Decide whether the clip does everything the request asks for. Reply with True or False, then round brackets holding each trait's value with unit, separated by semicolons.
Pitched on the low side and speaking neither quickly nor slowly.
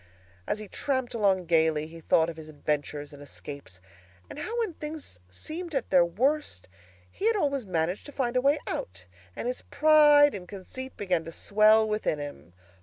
False (205 Hz; 180 wpm)